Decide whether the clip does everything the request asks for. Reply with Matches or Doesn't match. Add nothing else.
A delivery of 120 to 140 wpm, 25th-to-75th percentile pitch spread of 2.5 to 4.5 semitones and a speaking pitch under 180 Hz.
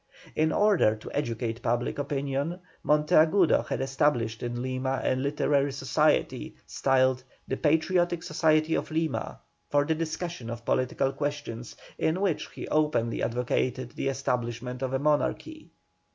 Matches